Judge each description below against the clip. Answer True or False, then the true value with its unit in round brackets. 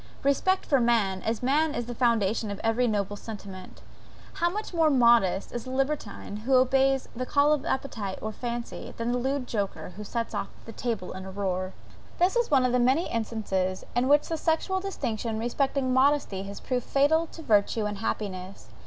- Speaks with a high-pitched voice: True (240 Hz)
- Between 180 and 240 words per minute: True (190 wpm)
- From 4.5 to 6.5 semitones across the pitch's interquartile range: True (4.9 semitones)